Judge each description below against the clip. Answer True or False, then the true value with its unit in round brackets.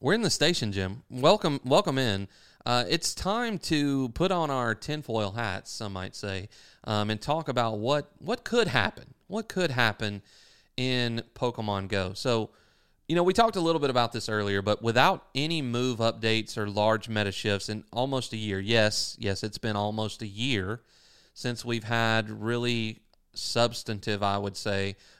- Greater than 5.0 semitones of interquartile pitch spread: False (4.4 semitones)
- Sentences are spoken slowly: False (175 wpm)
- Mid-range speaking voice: False (115 Hz)